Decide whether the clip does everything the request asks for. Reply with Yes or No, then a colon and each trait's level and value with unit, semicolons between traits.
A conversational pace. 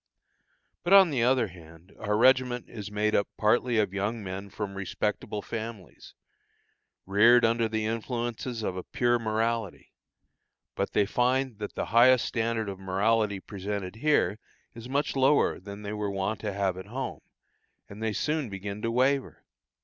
Yes: average, 160 wpm